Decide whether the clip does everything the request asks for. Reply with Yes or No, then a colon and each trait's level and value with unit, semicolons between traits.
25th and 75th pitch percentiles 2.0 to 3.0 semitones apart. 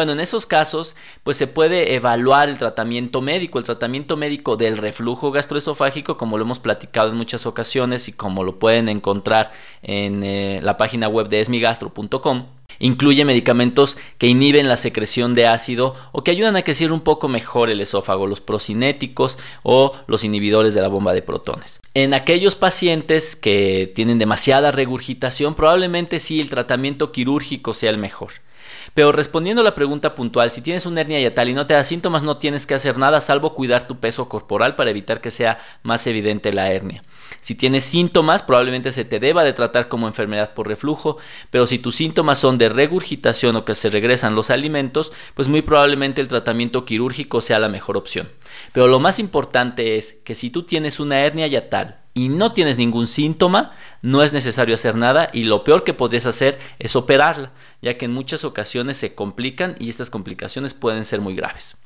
No: average, 4.3 semitones